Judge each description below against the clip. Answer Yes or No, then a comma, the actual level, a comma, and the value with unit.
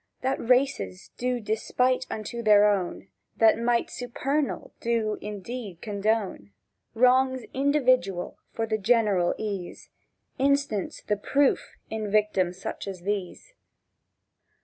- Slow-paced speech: Yes, slow, 110 wpm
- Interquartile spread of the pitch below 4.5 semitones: Yes, average, 3.9 semitones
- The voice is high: Yes, high, 220 Hz